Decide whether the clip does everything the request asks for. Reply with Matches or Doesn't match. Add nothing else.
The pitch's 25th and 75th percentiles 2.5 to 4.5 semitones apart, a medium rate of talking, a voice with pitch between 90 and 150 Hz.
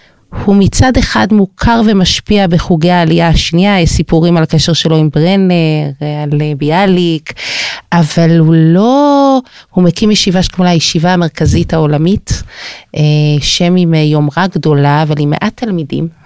Doesn't match